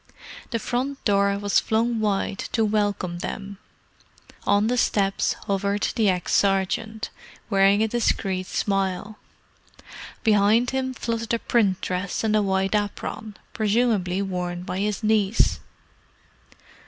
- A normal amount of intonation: No, narrow, 2.3 semitones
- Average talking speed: No, slow, 125 wpm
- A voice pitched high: Yes, high, 205 Hz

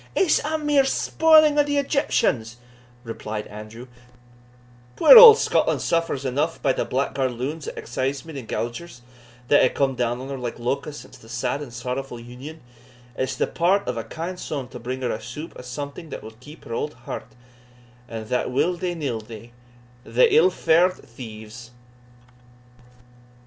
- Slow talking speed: No, average, 170 wpm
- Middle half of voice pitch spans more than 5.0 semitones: Yes, wide, 5.6 semitones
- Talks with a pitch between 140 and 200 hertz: No, low, 130 Hz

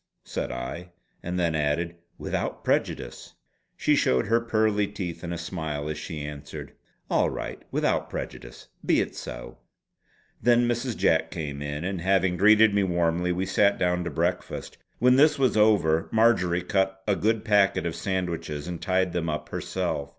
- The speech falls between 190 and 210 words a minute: No, average, 165 wpm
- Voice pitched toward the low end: Yes, very low, 90 Hz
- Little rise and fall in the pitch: No, average, 4.2 semitones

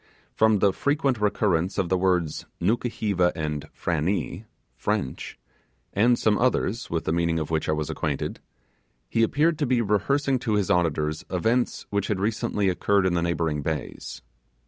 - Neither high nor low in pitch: No, very low, 95 Hz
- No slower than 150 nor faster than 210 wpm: Yes, average, 160 wpm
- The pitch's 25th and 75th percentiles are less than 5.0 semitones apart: No, average, 5.3 semitones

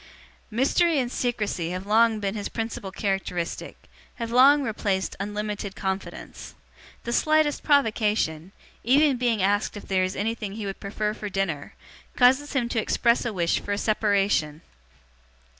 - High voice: Yes, high, 210 Hz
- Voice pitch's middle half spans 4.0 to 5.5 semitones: No, average, 3.6 semitones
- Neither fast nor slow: Yes, average, 145 wpm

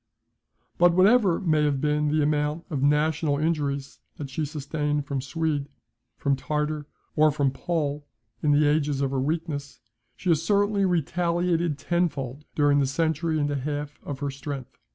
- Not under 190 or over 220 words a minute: No, average, 165 wpm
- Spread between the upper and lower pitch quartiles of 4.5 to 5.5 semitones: No, narrow, 2.4 semitones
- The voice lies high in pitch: No, medium, 150 Hz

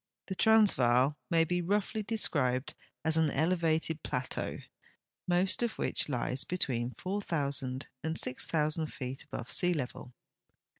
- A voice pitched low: No, medium, 155 Hz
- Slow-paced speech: Yes, slow, 120 wpm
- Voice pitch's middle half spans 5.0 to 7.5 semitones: Yes, wide, 5.6 semitones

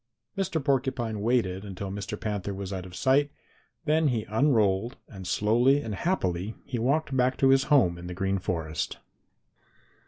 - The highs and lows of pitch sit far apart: Yes, wide, 5.8 semitones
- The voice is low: Yes, low, 110 Hz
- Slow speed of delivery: No, average, 160 wpm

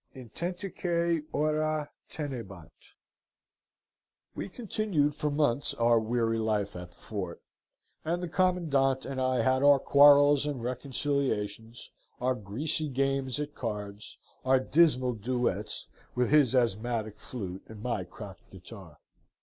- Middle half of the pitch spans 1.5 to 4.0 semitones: No, average, 5.0 semitones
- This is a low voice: Yes, low, 130 Hz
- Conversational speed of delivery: No, slow, 120 wpm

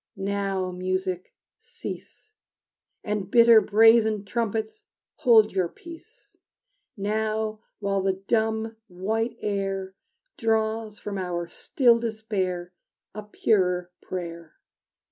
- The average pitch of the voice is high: Yes, high, 210 Hz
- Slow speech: Yes, slow, 95 wpm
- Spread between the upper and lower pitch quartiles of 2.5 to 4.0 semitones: Yes, average, 2.9 semitones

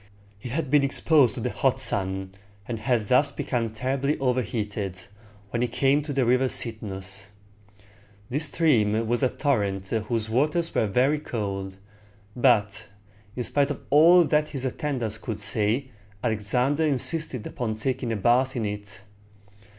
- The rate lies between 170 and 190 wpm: No, average, 150 wpm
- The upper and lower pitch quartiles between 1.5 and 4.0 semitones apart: No, average, 4.7 semitones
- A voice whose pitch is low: Yes, low, 120 Hz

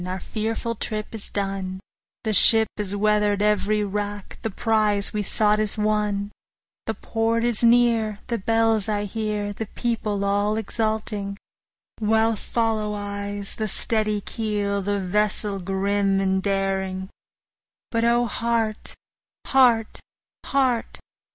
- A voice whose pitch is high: Yes, high, 210 Hz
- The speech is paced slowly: Yes, slow, 125 wpm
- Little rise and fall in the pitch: Yes, narrow, 1.7 semitones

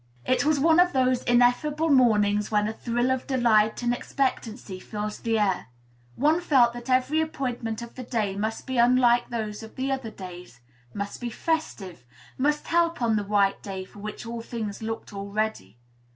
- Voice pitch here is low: No, high, 235 Hz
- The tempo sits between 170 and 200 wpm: Yes, average, 175 wpm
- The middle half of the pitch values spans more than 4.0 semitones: No, average, 3.7 semitones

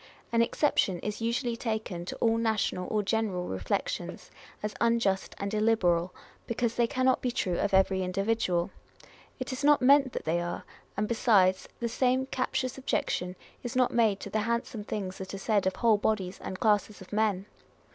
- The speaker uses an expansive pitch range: No, average, 3.7 semitones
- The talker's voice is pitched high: Yes, high, 215 Hz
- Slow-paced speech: No, average, 175 wpm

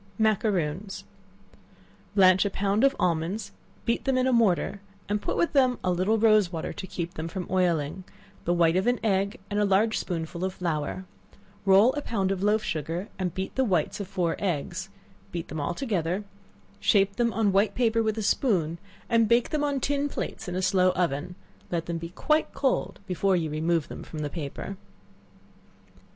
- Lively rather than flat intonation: No, average, 4.2 semitones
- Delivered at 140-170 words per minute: No, average, 190 wpm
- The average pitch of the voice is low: No, high, 190 Hz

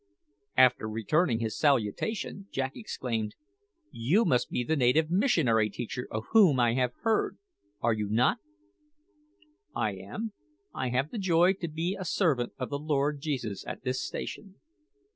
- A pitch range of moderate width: No, wide, 6.5 semitones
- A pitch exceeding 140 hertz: No, low, 135 Hz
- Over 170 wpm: No, average, 150 wpm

